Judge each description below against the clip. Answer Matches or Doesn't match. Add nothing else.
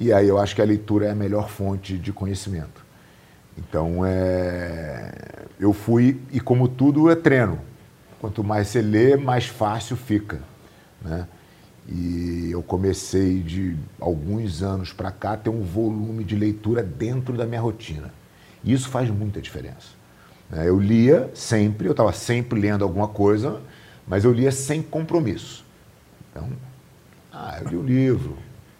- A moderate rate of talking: Matches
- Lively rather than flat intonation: Doesn't match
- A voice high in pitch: Doesn't match